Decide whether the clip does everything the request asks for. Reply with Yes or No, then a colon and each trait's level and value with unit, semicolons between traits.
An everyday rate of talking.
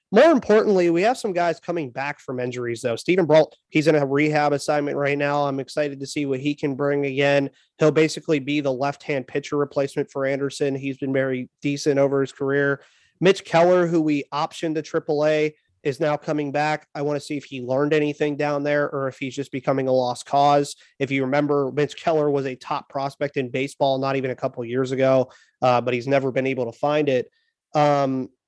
No: fast, 215 wpm